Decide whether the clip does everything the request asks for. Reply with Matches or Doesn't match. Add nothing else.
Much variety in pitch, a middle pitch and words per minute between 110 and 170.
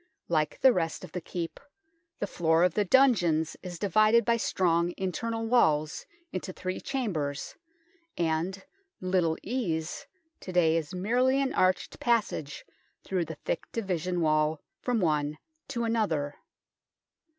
Matches